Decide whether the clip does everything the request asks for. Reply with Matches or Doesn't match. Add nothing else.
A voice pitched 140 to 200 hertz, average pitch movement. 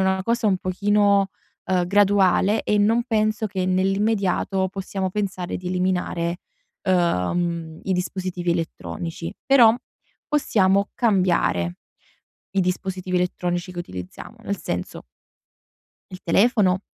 Doesn't match